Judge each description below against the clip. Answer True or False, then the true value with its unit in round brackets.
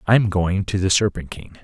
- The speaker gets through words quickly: True (255 wpm)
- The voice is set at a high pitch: False (95 Hz)